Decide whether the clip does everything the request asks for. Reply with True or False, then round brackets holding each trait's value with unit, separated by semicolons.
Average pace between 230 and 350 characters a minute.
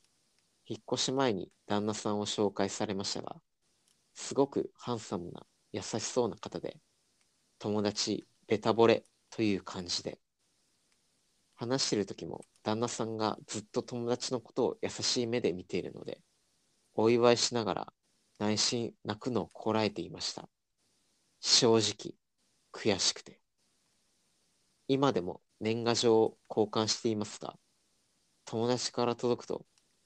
True (255 characters per minute)